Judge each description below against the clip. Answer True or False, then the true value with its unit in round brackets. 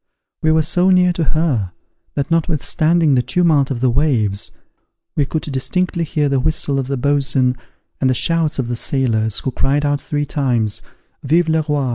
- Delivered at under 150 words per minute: False (180 wpm)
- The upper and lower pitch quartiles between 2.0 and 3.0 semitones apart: False (3.6 semitones)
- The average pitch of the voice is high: False (145 Hz)